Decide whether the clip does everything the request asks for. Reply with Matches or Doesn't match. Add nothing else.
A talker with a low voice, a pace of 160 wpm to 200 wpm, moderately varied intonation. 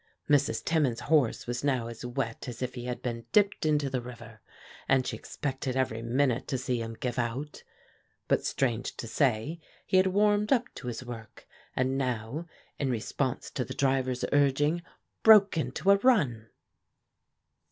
Matches